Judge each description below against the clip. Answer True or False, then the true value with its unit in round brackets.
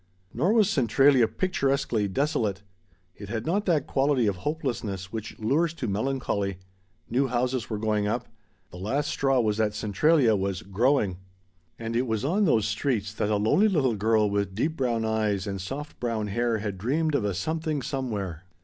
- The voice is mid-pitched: False (115 Hz)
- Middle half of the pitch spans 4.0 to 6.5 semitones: True (5.1 semitones)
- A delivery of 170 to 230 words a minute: True (175 wpm)